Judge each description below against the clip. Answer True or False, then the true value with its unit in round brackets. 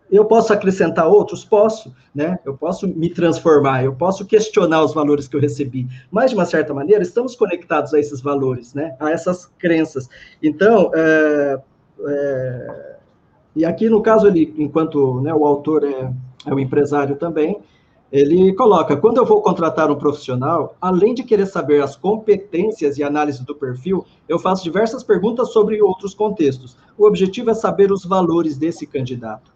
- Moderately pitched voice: True (160 Hz)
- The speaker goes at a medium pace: True (165 wpm)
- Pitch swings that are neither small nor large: False (5.9 semitones)